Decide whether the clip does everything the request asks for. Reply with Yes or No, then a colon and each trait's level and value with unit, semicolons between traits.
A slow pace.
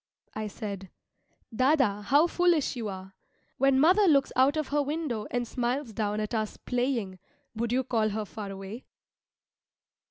No: average, 155 wpm